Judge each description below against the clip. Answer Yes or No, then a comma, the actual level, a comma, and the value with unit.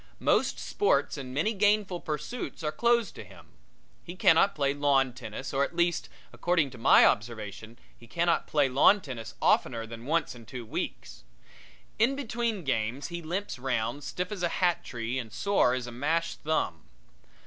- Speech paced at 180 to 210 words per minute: No, average, 170 wpm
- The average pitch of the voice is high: No, medium, 145 Hz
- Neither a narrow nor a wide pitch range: No, wide, 6.5 semitones